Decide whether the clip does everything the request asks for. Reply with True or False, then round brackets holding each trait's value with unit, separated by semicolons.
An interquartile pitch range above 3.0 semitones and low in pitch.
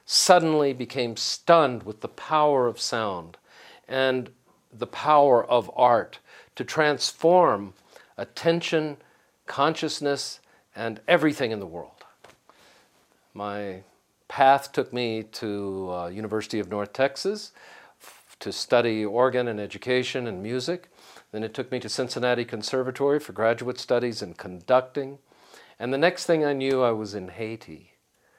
True (4.7 semitones; 125 Hz)